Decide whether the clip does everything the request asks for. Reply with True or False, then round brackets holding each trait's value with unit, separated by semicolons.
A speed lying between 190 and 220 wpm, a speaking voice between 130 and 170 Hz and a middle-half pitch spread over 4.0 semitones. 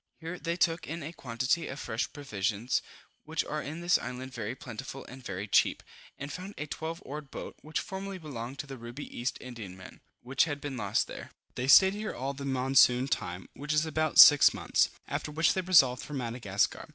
True (200 wpm; 140 Hz; 4.4 semitones)